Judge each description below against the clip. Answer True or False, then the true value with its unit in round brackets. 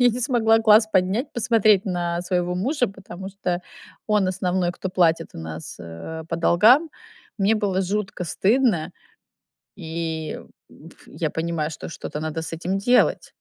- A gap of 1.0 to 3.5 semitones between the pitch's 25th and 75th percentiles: False (4.3 semitones)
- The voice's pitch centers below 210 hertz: True (185 Hz)